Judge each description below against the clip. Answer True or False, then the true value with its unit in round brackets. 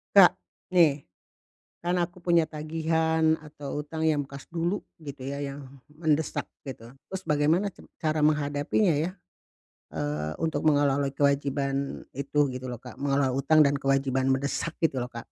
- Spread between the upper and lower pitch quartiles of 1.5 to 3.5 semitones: True (2.6 semitones)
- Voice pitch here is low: False (145 Hz)